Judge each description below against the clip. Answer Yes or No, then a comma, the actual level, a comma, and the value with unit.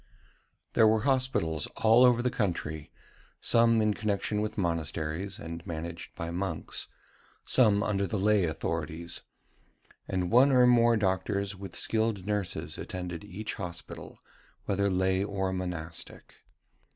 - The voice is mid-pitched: No, low, 100 Hz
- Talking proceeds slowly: Yes, slow, 125 wpm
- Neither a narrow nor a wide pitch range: Yes, average, 4.1 semitones